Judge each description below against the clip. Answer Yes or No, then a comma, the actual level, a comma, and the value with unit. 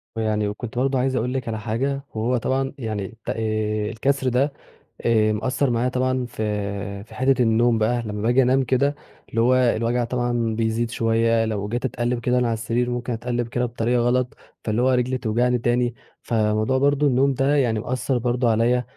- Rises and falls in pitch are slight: Yes, narrow, 2.2 semitones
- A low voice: Yes, low, 120 Hz